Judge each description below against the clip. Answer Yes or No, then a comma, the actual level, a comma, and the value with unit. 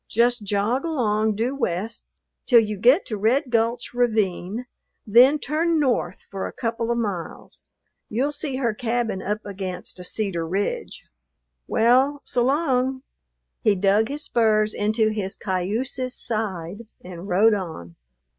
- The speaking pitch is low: No, high, 225 Hz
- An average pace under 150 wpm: Yes, average, 140 wpm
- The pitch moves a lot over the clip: No, average, 3.9 semitones